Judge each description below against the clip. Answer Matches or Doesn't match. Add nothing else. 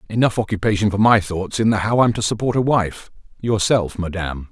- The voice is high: Doesn't match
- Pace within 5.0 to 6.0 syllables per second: Matches